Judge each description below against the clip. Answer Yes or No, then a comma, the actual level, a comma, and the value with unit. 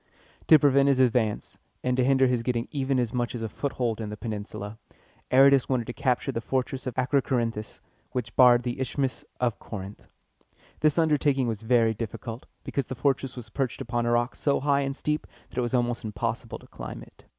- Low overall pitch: Yes, low, 125 Hz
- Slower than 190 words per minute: No, fast, 205 wpm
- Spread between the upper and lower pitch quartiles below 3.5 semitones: Yes, average, 2.7 semitones